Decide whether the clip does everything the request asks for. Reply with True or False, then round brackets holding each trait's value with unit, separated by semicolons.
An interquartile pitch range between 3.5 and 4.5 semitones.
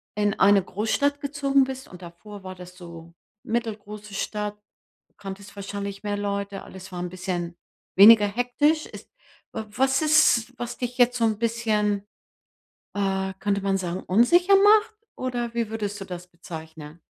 True (4.0 semitones)